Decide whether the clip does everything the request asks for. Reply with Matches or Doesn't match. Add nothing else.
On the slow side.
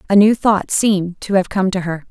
Doesn't match